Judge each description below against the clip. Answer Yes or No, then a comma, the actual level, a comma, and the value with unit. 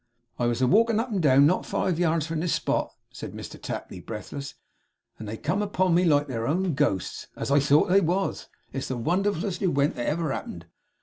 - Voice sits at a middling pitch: Yes, medium, 155 Hz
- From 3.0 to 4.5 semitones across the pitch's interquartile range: No, wide, 5.4 semitones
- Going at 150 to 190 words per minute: No, fast, 205 wpm